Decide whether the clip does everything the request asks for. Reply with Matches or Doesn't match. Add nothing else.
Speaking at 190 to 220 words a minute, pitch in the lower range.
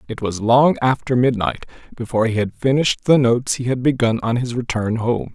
Matches